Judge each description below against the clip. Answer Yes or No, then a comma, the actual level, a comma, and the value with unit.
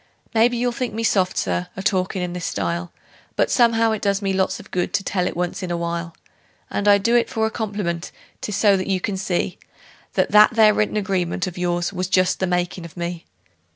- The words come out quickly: Yes, fast, 225 wpm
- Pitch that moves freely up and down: No, average, 3.2 semitones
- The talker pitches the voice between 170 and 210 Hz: Yes, high, 190 Hz